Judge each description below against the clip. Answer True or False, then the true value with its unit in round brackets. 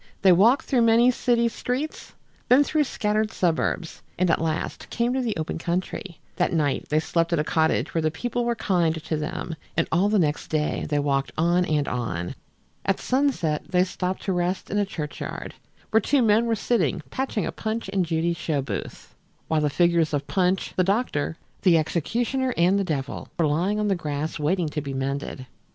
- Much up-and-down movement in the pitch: True (5.7 semitones)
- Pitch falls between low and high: True (175 Hz)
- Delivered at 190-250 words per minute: True (200 wpm)